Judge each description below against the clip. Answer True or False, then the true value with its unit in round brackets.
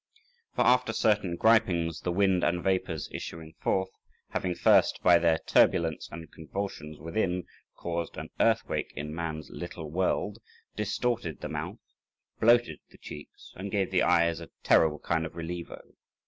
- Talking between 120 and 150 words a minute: True (145 wpm)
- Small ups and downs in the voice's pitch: False (3.0 semitones)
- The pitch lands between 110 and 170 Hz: False (85 Hz)